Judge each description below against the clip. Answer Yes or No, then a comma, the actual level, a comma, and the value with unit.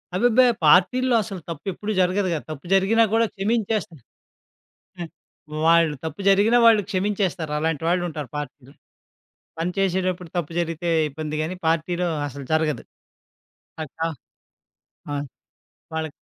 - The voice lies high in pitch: No, medium, 175 Hz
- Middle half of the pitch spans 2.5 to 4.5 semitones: Yes, average, 4.0 semitones